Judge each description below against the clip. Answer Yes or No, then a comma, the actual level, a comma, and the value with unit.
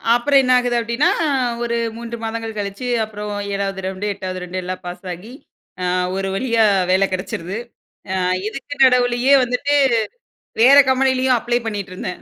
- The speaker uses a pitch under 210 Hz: No, high, 225 Hz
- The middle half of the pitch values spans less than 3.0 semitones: No, average, 4.4 semitones